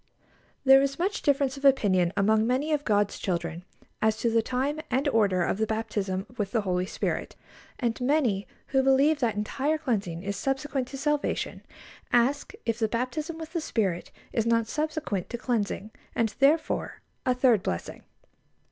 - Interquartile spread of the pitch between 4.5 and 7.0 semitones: Yes, average, 5.2 semitones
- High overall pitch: Yes, high, 240 Hz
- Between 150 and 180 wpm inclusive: Yes, average, 165 wpm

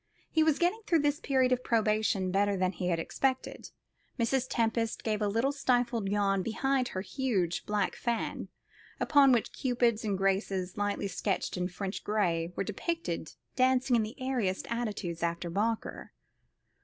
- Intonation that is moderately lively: Yes, average, 4.8 semitones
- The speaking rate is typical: Yes, average, 155 wpm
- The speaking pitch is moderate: No, high, 220 Hz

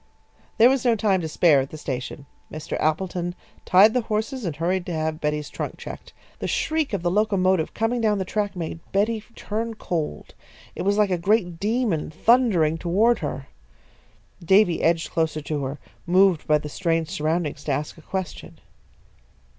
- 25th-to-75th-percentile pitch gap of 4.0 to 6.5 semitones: Yes, average, 5.2 semitones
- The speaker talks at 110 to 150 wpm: No, average, 175 wpm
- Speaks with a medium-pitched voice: Yes, medium, 180 Hz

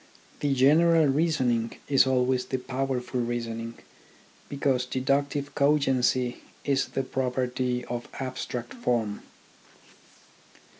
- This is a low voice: Yes, low, 130 Hz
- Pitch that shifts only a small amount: Yes, narrow, 2.1 semitones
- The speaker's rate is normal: No, slow, 100 wpm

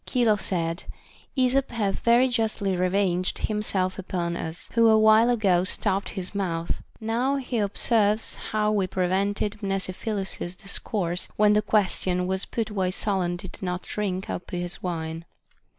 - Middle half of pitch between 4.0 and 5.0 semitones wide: No, average, 3.0 semitones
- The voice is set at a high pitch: Yes, high, 195 Hz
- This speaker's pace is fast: No, average, 140 wpm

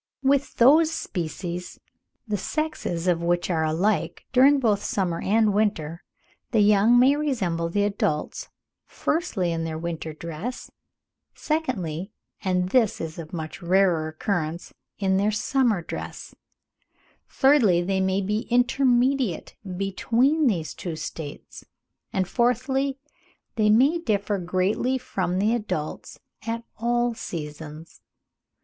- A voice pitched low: No, high, 200 Hz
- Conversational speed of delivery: No, slow, 125 wpm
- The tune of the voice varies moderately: No, wide, 6.1 semitones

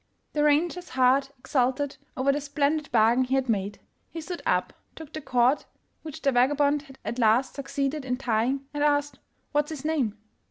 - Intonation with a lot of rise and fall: No, average, 2.8 semitones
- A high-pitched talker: Yes, very high, 275 Hz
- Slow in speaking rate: No, average, 185 wpm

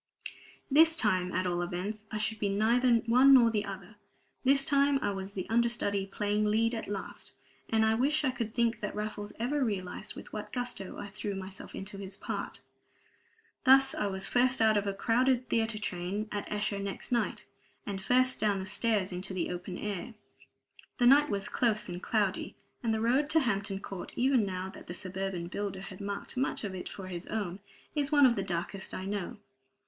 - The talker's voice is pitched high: Yes, high, 210 Hz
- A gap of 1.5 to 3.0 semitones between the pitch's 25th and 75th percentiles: No, average, 3.7 semitones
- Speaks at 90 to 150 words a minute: No, average, 195 wpm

